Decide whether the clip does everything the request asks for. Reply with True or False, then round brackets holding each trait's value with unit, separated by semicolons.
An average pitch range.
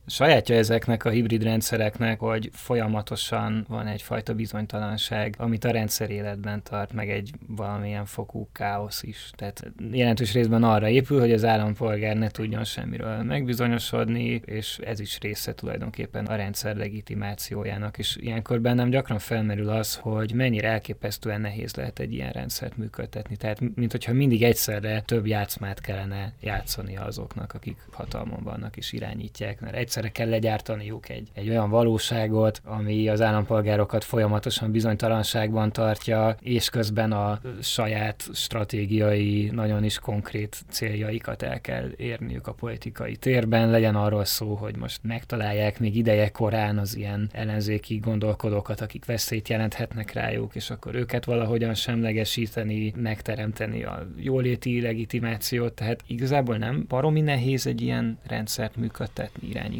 False (1.6 semitones)